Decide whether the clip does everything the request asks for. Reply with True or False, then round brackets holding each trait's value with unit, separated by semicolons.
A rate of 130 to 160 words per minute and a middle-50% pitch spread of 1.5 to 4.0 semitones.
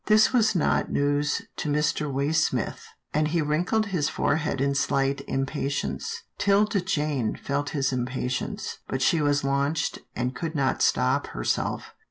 True (145 wpm; 3.3 semitones)